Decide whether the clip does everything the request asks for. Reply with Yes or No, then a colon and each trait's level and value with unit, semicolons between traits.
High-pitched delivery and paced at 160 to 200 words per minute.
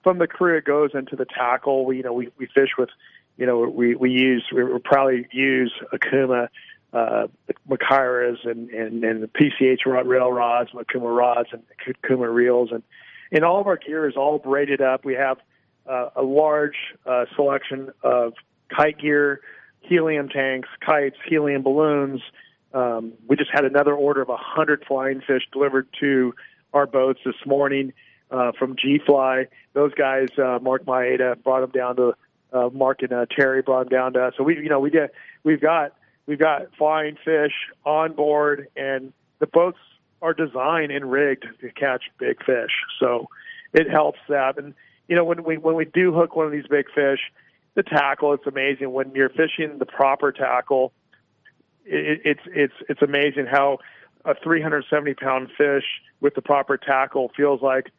No: low, 135 Hz; average, 180 wpm